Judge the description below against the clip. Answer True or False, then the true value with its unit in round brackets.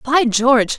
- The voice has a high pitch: True (250 Hz)